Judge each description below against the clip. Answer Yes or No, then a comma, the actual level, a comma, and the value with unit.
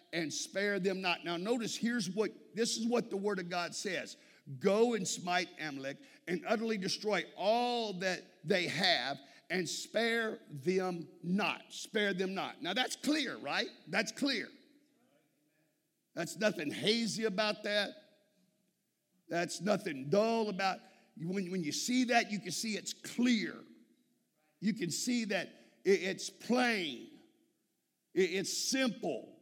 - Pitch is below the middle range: No, high, 205 Hz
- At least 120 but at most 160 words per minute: Yes, slow, 135 wpm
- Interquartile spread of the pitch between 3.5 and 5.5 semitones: Yes, average, 4.2 semitones